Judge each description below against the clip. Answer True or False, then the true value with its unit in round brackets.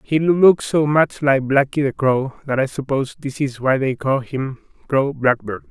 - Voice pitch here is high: False (135 Hz)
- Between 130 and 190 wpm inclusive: False (200 wpm)